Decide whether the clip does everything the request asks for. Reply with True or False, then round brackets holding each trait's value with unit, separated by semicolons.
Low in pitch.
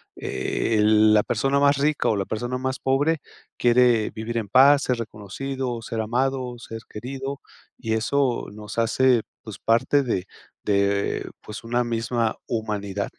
True (115 Hz)